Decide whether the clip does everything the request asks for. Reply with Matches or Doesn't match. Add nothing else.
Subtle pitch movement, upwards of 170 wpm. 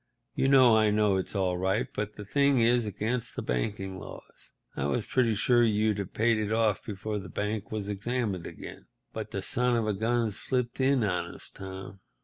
Doesn't match